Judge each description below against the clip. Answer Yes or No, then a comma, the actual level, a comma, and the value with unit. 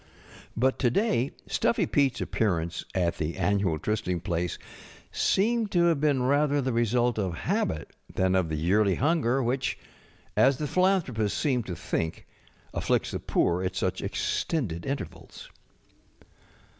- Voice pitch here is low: Yes, low, 115 Hz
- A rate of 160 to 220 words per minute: No, average, 145 wpm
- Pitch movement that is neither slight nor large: No, wide, 7.5 semitones